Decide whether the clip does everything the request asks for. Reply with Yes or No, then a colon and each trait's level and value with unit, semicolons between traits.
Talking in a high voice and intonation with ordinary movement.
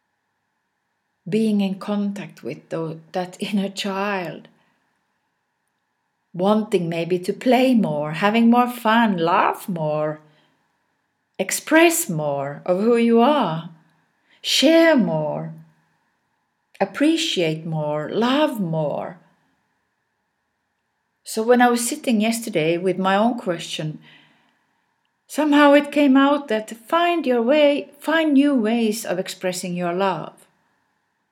No: high, 205 Hz; wide, 6.4 semitones